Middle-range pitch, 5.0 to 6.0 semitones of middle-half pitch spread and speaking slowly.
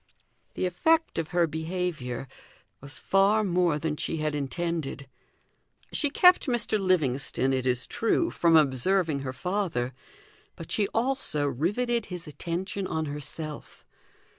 Yes: medium, 165 Hz; average, 5.3 semitones; slow, 130 wpm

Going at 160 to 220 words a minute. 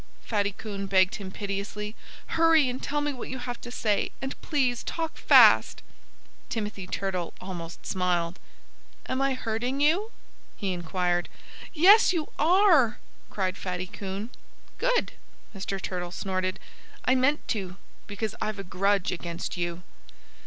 No: average, 140 wpm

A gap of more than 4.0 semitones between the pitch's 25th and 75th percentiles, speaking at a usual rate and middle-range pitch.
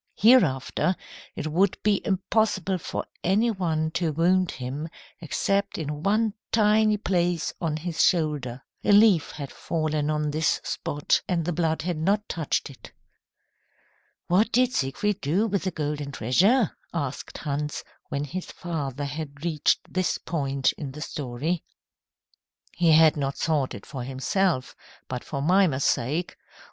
Yes: average, 4.4 semitones; average, 145 wpm; medium, 160 Hz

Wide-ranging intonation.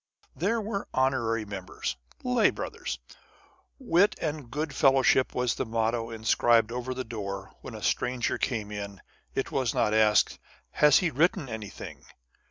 No: average, 5.0 semitones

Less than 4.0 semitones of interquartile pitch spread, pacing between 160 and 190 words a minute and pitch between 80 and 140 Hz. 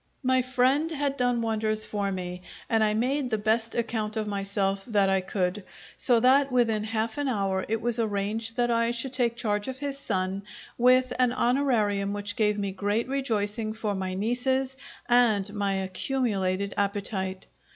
No: average, 3.6 semitones; average, 170 wpm; high, 220 Hz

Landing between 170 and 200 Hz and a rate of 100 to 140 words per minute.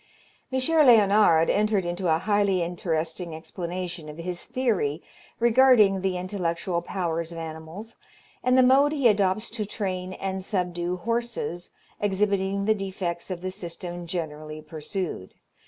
Yes: medium, 185 Hz; slow, 135 wpm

